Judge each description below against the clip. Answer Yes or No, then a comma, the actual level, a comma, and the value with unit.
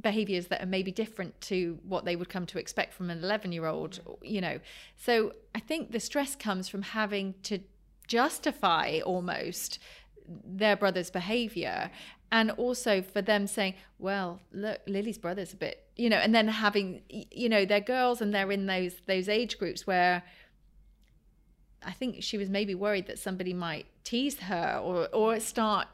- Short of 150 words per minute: No, average, 175 wpm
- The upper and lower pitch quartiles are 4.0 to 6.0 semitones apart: No, average, 2.9 semitones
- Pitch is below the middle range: No, high, 200 Hz